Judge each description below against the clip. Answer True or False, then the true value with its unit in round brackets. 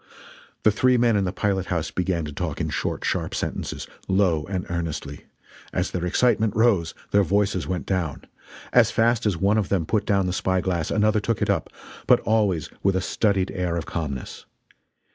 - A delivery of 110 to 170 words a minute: False (190 wpm)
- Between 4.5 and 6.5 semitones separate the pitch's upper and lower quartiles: False (3.3 semitones)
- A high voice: False (95 Hz)